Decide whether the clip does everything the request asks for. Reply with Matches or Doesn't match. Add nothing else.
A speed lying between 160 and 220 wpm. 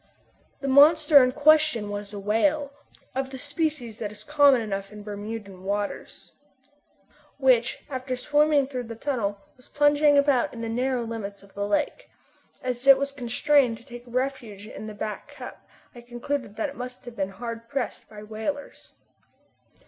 Matches